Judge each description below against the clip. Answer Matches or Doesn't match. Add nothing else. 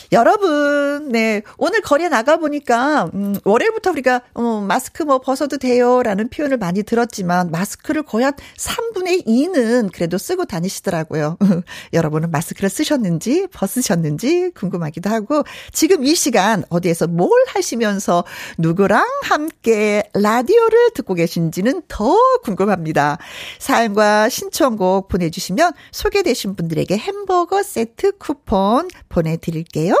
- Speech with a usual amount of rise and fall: Doesn't match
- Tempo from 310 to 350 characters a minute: Matches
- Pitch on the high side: Matches